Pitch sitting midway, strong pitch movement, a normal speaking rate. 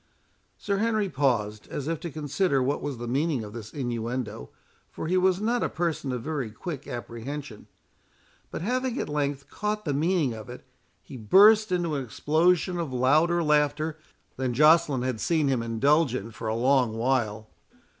Yes: medium, 145 Hz; wide, 5.7 semitones; average, 175 wpm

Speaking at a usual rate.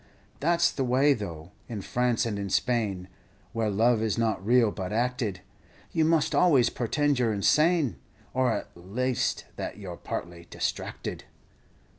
Yes: average, 155 wpm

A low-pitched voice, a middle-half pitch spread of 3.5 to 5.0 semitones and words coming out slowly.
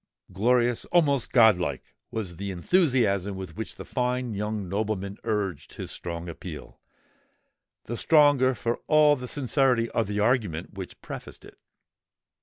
Yes: low, 110 Hz; average, 4.6 semitones; slow, 130 wpm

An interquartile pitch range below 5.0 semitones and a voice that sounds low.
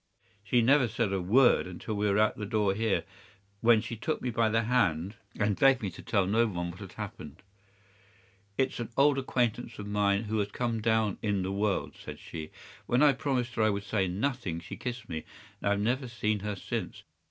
Yes: average, 3.3 semitones; low, 110 Hz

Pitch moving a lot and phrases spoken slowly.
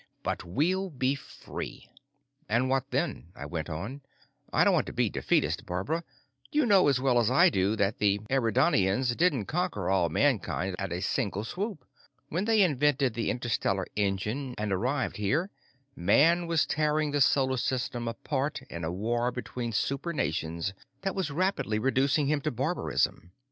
No: wide, 6.5 semitones; average, 165 wpm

